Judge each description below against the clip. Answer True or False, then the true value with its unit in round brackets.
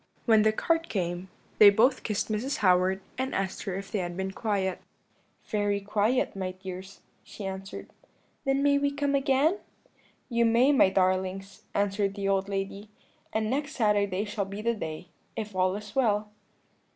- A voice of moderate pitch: False (205 Hz)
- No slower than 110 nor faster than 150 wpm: False (165 wpm)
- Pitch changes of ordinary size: True (3.4 semitones)